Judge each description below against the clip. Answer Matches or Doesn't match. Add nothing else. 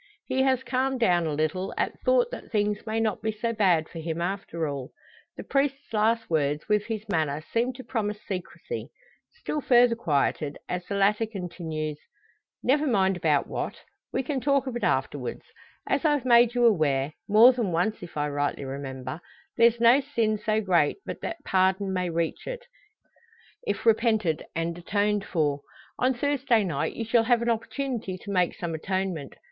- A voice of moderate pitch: Doesn't match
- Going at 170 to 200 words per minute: Matches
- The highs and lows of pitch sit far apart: Matches